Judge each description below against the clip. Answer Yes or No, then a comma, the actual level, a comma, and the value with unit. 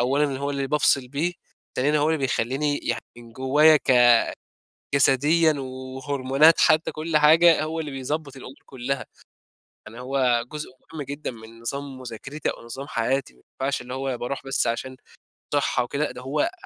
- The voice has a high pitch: No, low, 135 Hz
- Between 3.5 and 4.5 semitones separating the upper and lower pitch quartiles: No, average, 2.8 semitones